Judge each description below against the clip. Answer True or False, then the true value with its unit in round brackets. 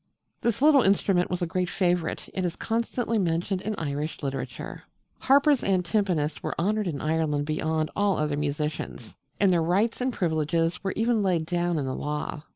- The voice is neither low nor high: True (175 Hz)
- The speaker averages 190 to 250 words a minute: False (175 wpm)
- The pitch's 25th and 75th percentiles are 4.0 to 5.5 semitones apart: True (4.6 semitones)